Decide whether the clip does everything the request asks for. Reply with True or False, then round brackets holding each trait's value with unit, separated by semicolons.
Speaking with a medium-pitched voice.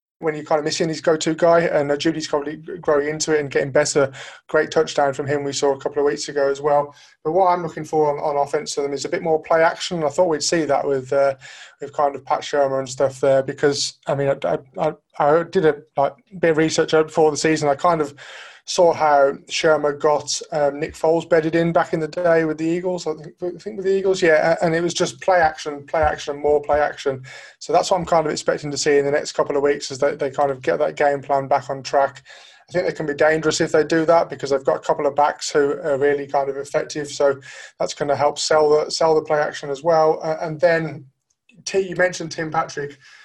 True (150 Hz)